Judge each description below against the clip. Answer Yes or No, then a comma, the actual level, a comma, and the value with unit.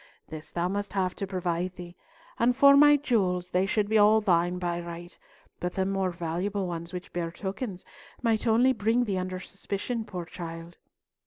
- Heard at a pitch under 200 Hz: Yes, medium, 185 Hz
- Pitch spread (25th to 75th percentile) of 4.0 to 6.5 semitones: No, average, 3.4 semitones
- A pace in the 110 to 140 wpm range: No, average, 180 wpm